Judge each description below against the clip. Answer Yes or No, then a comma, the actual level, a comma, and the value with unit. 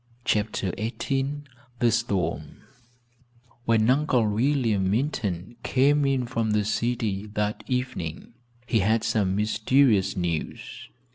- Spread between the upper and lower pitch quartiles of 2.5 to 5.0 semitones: Yes, average, 3.9 semitones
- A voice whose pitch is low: Yes, low, 110 Hz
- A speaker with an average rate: No, slow, 110 wpm